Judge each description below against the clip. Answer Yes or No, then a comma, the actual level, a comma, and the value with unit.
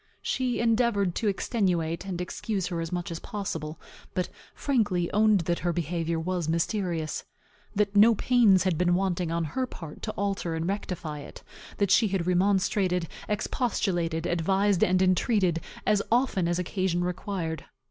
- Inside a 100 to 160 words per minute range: Yes, average, 155 wpm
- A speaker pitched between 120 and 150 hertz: No, medium, 185 Hz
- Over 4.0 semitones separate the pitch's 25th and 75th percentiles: No, average, 3.2 semitones